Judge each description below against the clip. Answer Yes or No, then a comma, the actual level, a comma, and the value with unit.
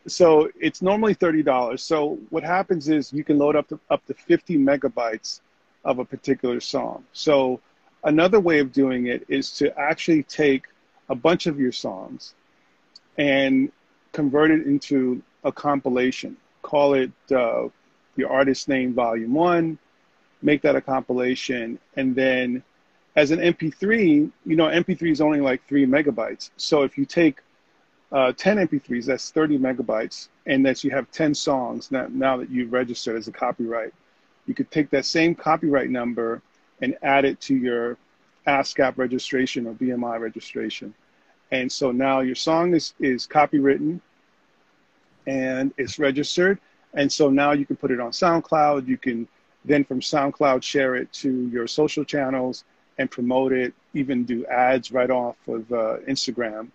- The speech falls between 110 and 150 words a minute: No, average, 160 wpm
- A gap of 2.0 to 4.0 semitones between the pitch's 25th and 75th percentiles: Yes, average, 3.3 semitones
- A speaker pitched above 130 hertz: Yes, medium, 140 Hz